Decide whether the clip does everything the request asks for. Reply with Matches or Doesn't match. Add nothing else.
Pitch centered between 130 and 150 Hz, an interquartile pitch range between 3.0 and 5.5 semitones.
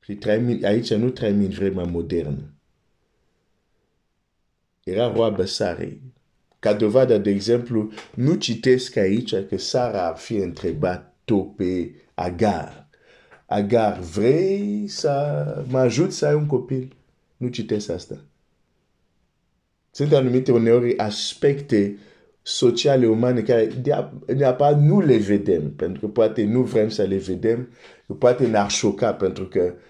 Doesn't match